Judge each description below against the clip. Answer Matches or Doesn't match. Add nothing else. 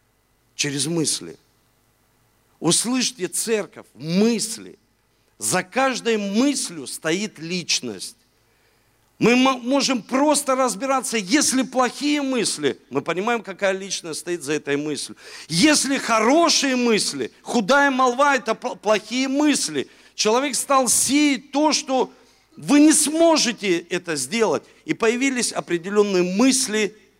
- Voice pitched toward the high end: Matches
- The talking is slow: Matches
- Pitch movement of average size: Doesn't match